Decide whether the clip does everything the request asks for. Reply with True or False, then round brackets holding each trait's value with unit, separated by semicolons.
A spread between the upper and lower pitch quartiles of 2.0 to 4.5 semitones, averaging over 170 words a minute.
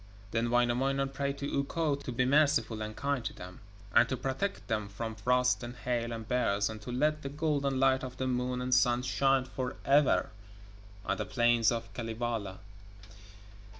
True (2.9 semitones; 180 wpm)